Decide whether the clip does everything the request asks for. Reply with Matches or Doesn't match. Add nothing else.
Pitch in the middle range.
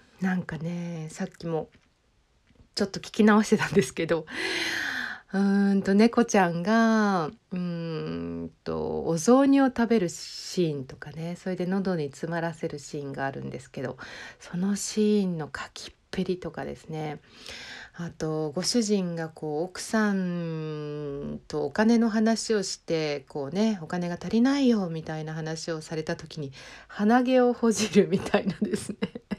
Matches